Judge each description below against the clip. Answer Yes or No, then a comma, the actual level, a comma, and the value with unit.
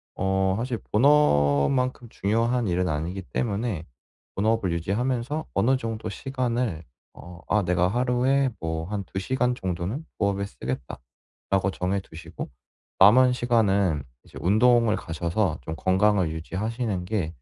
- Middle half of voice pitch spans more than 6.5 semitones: No, average, 5.3 semitones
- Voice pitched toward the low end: Yes, low, 100 Hz